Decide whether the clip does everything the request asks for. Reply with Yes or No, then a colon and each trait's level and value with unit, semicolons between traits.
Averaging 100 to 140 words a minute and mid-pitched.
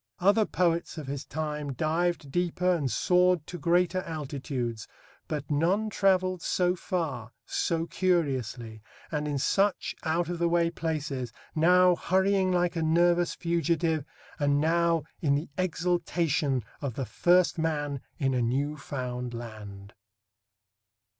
Yes: slow, 135 wpm; medium, 160 Hz